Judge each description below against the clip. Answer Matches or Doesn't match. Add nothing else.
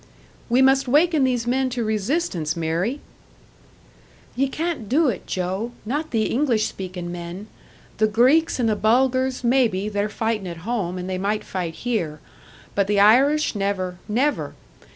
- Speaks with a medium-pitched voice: Doesn't match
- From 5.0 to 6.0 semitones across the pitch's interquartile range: Matches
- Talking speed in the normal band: Matches